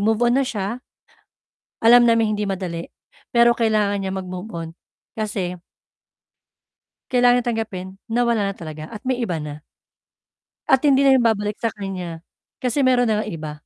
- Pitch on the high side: Yes, high, 215 Hz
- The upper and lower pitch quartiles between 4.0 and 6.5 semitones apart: Yes, average, 4.3 semitones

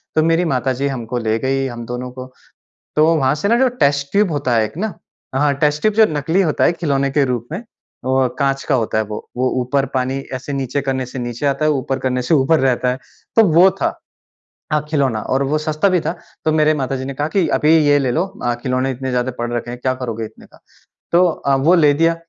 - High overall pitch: No, low, 135 Hz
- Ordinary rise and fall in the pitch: Yes, average, 3.2 semitones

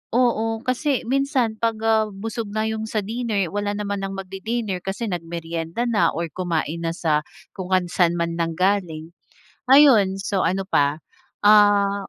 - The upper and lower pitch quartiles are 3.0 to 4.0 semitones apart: No, average, 4.4 semitones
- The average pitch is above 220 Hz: No, high, 200 Hz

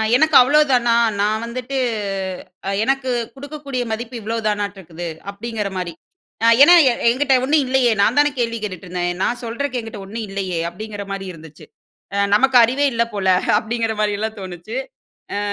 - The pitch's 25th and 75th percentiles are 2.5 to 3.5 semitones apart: No, average, 4.2 semitones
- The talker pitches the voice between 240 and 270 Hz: No, high, 225 Hz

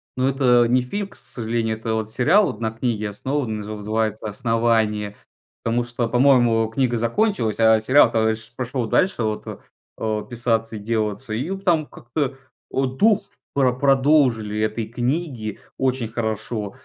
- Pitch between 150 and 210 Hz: No, low, 115 Hz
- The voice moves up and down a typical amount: Yes, average, 3.1 semitones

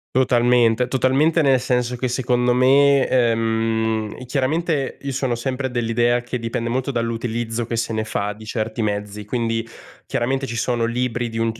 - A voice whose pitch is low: Yes, low, 120 Hz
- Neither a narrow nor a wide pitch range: No, narrow, 2.2 semitones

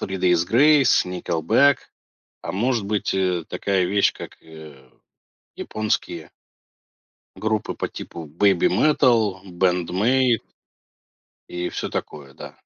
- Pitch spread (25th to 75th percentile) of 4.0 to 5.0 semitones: Yes, average, 4.5 semitones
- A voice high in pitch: No, very low, 95 Hz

